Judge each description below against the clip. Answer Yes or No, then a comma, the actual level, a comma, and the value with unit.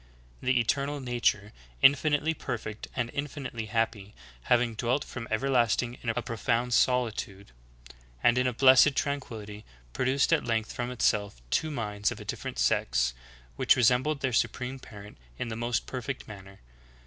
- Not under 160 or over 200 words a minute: No, average, 150 wpm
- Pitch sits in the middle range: No, low, 120 Hz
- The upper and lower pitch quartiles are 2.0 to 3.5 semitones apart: Yes, average, 3.2 semitones